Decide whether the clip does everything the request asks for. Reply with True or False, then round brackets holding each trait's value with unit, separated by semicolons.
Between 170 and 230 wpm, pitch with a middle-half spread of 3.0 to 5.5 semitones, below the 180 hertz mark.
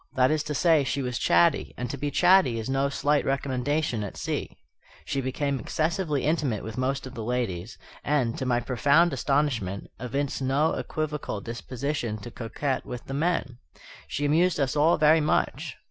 True (175 wpm; 3.4 semitones; 135 Hz)